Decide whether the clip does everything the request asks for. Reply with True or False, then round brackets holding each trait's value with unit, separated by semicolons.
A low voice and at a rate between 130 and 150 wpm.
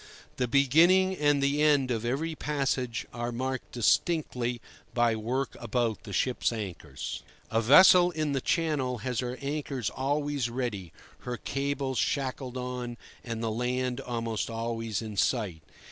True (125 Hz; 145 wpm)